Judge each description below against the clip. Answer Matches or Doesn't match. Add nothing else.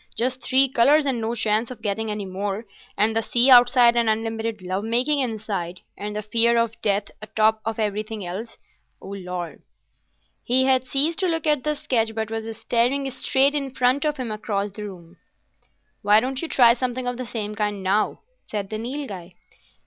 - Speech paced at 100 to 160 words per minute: Doesn't match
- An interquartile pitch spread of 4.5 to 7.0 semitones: Doesn't match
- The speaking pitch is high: Matches